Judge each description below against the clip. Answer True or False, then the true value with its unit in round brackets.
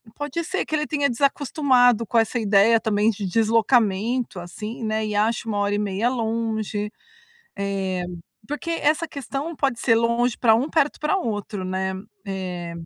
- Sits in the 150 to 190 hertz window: False (225 Hz)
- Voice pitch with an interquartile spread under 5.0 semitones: True (4.2 semitones)